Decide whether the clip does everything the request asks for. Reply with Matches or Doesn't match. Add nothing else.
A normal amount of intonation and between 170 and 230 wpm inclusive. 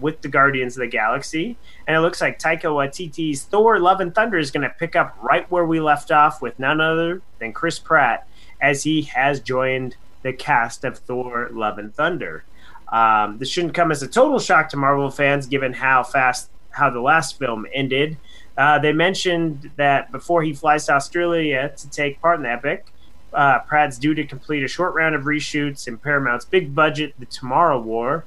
Matches